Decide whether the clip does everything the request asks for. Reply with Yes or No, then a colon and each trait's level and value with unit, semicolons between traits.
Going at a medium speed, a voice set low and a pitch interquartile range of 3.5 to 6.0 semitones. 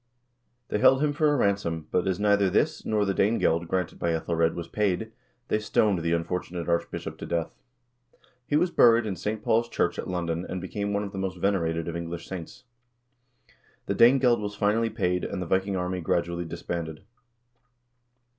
Yes: average, 180 wpm; very low, 95 Hz; average, 3.8 semitones